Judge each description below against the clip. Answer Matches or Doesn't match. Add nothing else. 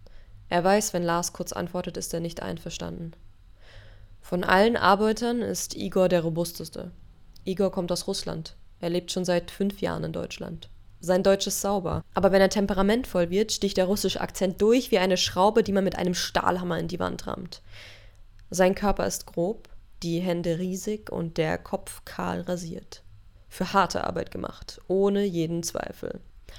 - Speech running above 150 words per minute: Matches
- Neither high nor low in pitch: Matches